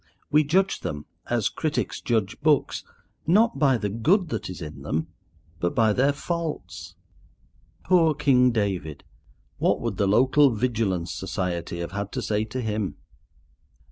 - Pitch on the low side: Yes, low, 110 Hz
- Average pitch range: No, wide, 7.6 semitones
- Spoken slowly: No, average, 145 wpm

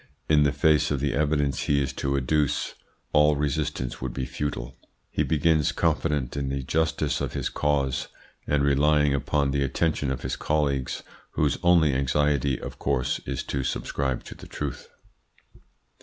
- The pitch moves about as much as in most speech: No, narrow, 1.8 semitones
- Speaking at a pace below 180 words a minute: Yes, average, 160 wpm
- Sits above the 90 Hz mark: No, very low, 70 Hz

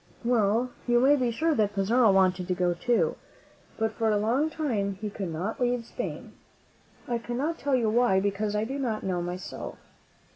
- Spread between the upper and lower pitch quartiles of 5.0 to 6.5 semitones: No, average, 3.9 semitones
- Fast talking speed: No, average, 185 wpm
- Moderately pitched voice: No, high, 225 Hz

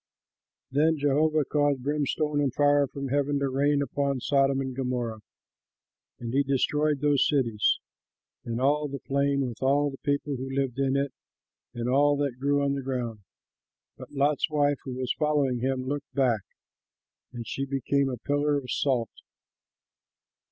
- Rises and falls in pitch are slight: Yes, narrow, 1.8 semitones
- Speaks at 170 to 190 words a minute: No, average, 160 wpm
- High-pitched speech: No, medium, 140 Hz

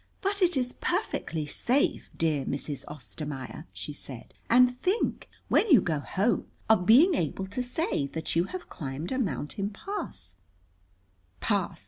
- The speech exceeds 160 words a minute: No, average, 145 wpm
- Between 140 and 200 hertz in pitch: Yes, high, 190 Hz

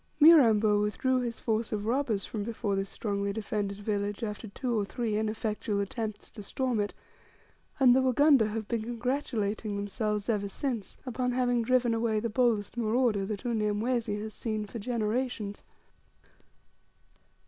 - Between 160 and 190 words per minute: No, average, 150 wpm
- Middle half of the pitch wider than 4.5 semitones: No, average, 2.8 semitones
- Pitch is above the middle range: Yes, high, 220 Hz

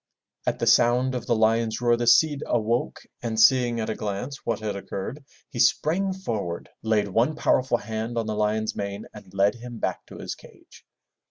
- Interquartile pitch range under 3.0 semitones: Yes, narrow, 2.4 semitones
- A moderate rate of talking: Yes, average, 190 wpm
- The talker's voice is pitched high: No, low, 115 Hz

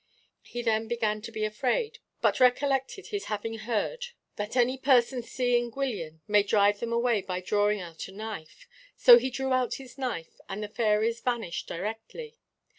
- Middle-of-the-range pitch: No, high, 230 Hz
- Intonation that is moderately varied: Yes, average, 3.3 semitones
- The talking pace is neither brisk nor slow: Yes, average, 170 wpm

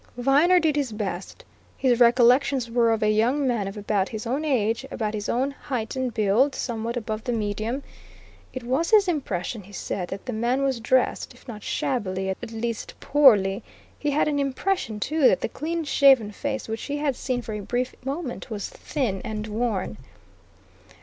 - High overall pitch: Yes, high, 240 Hz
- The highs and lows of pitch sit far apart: No, average, 4.3 semitones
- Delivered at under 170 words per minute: No, average, 185 wpm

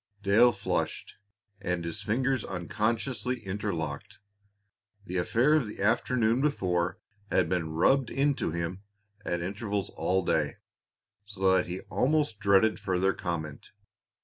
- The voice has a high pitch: No, low, 100 Hz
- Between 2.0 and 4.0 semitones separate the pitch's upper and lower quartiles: No, average, 4.8 semitones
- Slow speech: Yes, slow, 120 wpm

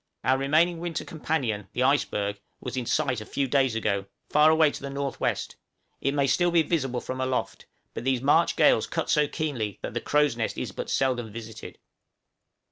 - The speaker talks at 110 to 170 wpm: No, average, 190 wpm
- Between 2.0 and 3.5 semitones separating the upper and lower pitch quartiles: No, average, 4.1 semitones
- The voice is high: No, low, 135 Hz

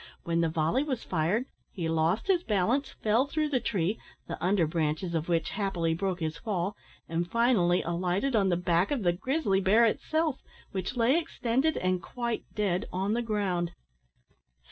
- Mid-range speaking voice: No, high, 195 Hz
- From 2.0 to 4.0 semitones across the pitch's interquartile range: No, wide, 5.5 semitones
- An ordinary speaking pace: Yes, average, 170 wpm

